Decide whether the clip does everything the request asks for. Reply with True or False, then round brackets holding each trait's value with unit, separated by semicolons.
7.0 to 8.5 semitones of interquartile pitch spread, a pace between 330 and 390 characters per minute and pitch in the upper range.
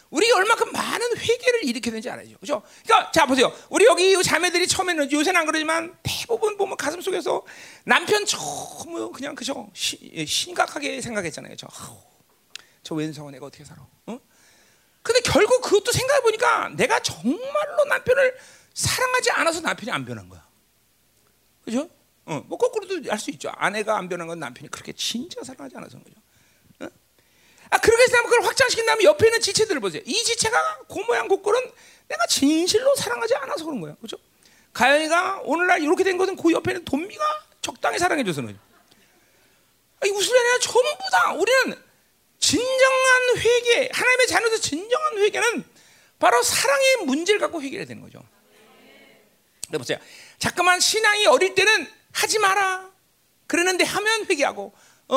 True (8.2 semitones; 355 characters per minute; 370 Hz)